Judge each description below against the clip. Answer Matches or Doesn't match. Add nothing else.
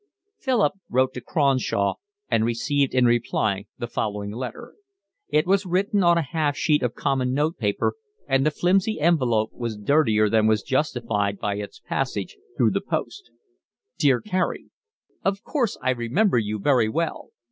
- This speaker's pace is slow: Doesn't match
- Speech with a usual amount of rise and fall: Doesn't match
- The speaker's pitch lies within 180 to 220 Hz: Doesn't match